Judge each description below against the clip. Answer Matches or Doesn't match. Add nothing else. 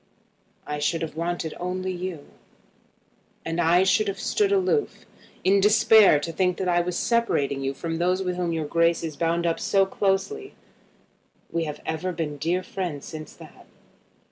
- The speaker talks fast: Doesn't match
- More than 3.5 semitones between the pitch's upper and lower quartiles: Doesn't match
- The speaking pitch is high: Doesn't match